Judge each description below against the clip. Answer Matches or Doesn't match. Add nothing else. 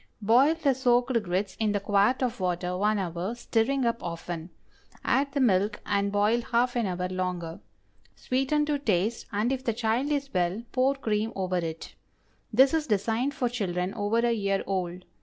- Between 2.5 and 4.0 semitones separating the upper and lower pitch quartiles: Doesn't match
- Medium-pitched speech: Doesn't match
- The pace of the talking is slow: Doesn't match